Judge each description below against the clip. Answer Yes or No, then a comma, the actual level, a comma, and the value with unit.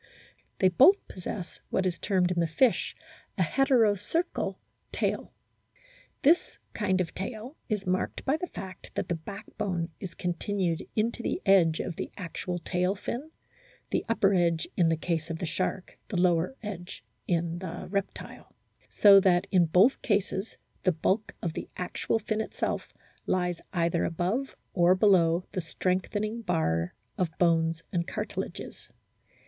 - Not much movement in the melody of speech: No, average, 3.3 semitones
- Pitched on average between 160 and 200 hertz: Yes, medium, 185 Hz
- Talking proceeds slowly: No, average, 155 wpm